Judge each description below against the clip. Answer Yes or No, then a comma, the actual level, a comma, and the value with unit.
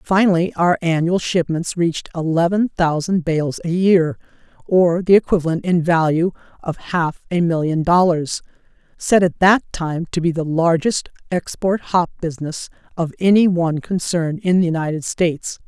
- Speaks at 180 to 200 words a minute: No, average, 145 wpm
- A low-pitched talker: No, medium, 170 Hz